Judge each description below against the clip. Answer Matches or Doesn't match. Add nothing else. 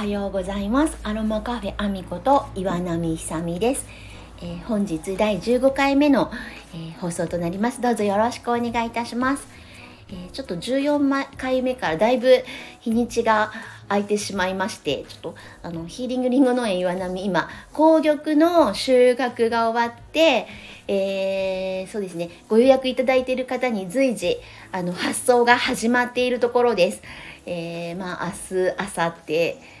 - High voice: Matches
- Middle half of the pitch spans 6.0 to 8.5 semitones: Doesn't match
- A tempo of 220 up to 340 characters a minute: Matches